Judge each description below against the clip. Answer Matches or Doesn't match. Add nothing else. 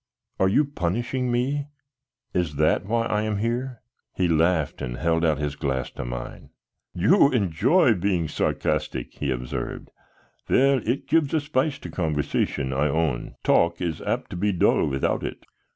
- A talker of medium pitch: Doesn't match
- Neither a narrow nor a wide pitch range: Doesn't match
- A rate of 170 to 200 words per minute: Doesn't match